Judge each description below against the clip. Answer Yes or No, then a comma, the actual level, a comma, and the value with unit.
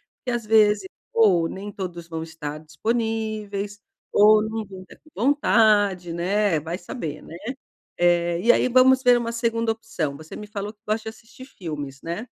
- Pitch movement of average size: Yes, average, 4.7 semitones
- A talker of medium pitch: No, high, 205 Hz